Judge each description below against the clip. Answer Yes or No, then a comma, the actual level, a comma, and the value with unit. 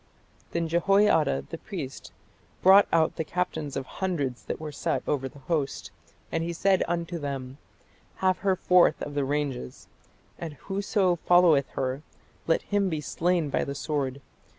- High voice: No, medium, 160 Hz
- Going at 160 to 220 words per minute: No, average, 150 wpm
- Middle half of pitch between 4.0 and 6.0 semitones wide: Yes, average, 4.3 semitones